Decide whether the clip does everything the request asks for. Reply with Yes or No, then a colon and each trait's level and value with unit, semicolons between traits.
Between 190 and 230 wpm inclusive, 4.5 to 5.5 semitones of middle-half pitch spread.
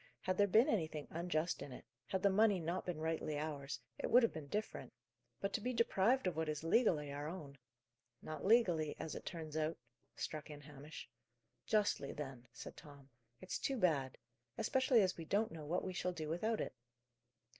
Yes: average, 195 wpm; average, 5.0 semitones